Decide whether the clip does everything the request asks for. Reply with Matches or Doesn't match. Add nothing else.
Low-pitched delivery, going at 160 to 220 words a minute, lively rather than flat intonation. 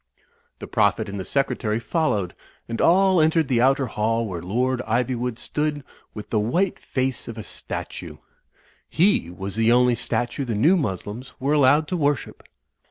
Doesn't match